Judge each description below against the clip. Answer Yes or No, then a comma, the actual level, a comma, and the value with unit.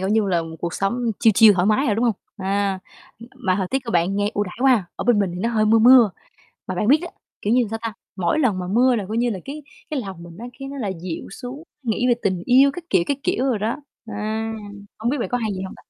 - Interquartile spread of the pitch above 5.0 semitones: No, average, 4.4 semitones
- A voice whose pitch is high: Yes, high, 220 Hz